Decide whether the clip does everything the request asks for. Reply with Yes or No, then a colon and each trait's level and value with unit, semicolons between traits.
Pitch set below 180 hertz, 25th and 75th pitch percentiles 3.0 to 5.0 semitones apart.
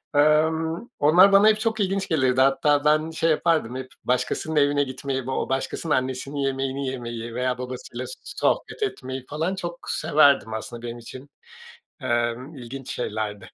Yes: low, 135 Hz; average, 3.9 semitones